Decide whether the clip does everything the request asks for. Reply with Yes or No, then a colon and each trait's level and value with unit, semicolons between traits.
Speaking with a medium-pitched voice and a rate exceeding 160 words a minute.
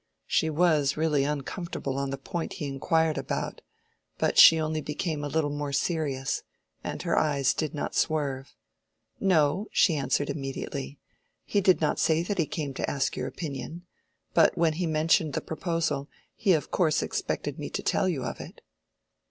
Yes: medium, 155 Hz; average, 170 wpm